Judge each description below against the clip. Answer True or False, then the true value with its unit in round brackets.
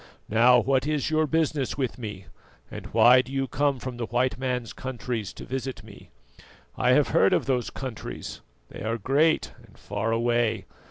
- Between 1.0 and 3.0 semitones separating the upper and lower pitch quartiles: True (2.7 semitones)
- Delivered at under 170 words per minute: False (175 wpm)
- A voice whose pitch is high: False (125 Hz)